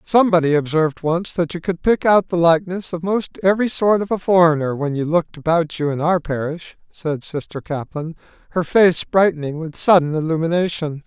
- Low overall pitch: No, medium, 165 Hz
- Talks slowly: No, average, 185 wpm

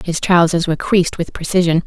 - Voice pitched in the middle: Yes, medium, 170 Hz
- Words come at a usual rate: Yes, average, 195 wpm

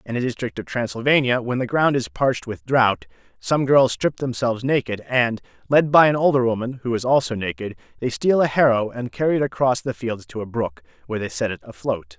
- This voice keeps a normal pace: No, fast, 220 wpm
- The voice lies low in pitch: Yes, low, 120 Hz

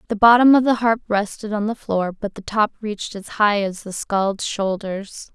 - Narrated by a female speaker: Yes, female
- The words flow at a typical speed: No, fast, 215 wpm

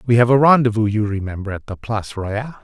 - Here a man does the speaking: Yes, male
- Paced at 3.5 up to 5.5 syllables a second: No, 6.4 syllables/s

